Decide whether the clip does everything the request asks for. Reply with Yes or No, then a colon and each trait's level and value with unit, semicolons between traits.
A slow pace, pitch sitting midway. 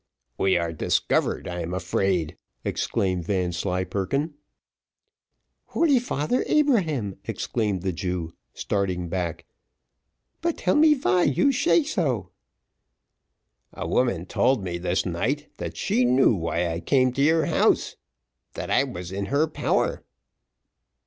No: slow, 120 wpm; low, 100 Hz